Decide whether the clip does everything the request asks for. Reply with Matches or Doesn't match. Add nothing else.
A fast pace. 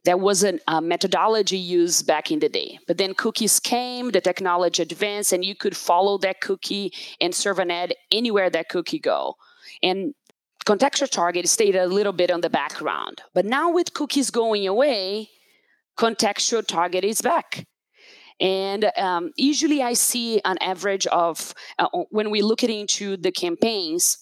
Doesn't match